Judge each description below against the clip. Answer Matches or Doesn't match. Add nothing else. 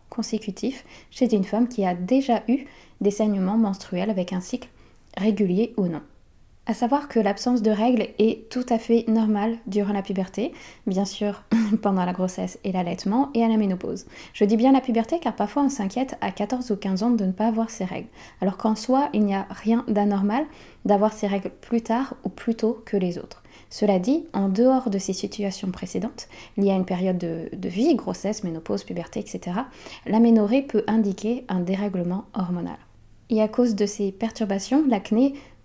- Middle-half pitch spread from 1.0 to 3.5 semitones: Matches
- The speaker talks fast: Doesn't match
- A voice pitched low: Doesn't match